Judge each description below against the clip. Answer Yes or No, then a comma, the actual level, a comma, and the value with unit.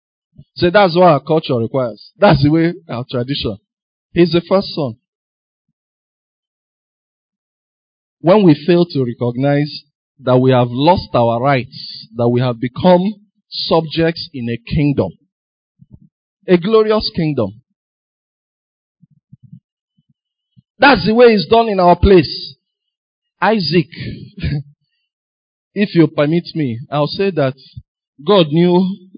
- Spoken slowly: Yes, slow, 115 wpm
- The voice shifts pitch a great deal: Yes, wide, 6.4 semitones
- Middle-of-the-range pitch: Yes, medium, 160 Hz